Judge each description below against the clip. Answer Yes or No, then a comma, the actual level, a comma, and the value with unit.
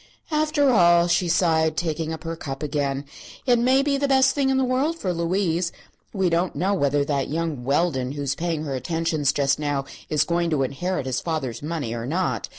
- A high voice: No, medium, 165 Hz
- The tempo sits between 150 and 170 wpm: No, fast, 205 wpm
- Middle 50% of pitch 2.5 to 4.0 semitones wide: No, average, 4.6 semitones